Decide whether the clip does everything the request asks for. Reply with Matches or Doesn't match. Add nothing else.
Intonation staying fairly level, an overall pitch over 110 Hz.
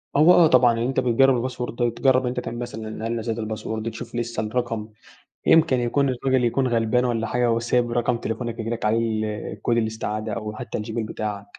Matches